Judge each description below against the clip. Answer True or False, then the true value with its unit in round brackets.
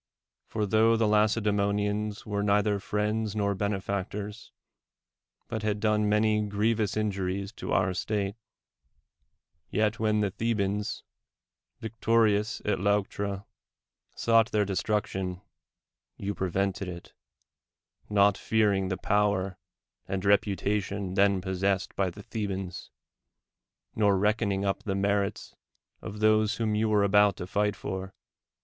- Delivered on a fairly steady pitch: True (1.5 semitones)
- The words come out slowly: True (120 wpm)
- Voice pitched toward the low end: True (105 Hz)